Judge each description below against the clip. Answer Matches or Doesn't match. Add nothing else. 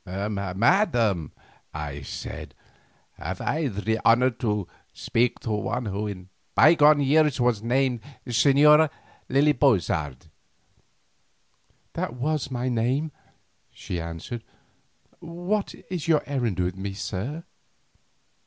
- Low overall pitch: Matches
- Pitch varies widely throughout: Matches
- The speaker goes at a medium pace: Doesn't match